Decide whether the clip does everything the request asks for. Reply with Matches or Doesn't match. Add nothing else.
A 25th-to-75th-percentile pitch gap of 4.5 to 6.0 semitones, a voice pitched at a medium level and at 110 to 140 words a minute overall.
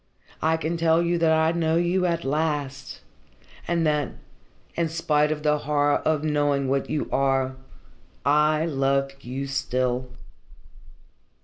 Doesn't match